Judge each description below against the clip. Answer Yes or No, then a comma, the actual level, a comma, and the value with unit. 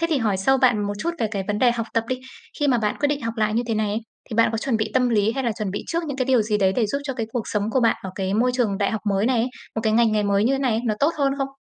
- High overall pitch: Yes, high, 225 Hz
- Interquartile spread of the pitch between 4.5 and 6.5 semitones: No, average, 3.4 semitones